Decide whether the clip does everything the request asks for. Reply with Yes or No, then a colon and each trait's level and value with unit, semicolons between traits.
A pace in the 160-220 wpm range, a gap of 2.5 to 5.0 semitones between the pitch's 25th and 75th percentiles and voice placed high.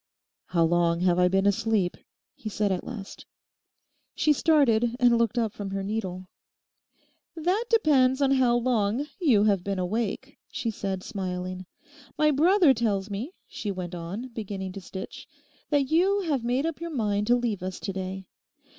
No: average, 165 wpm; wide, 5.5 semitones; high, 220 Hz